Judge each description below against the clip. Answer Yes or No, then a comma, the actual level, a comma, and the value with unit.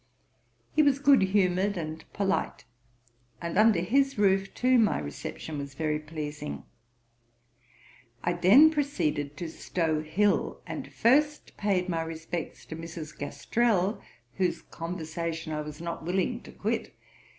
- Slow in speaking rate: Yes, slow, 130 wpm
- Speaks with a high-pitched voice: No, medium, 175 Hz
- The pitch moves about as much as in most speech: Yes, average, 4.8 semitones